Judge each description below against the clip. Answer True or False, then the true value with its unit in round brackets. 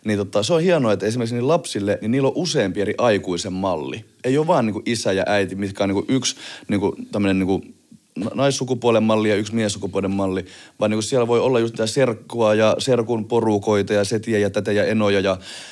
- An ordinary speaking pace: False (210 wpm)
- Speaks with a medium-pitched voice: False (105 Hz)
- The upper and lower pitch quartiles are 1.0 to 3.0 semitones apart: True (2.7 semitones)